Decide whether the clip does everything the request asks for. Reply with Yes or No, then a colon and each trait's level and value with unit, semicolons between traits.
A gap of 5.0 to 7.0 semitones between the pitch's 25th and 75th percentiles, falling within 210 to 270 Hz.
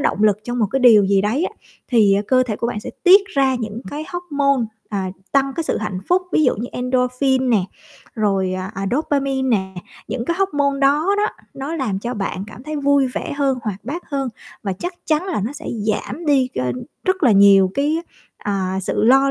Yes: wide, 5.4 semitones; very high, 255 Hz